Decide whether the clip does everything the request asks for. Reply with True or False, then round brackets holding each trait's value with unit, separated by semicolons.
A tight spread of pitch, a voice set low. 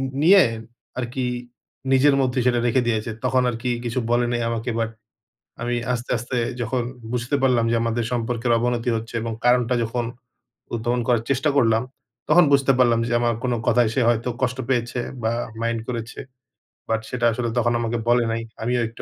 True (1.4 semitones; 120 Hz)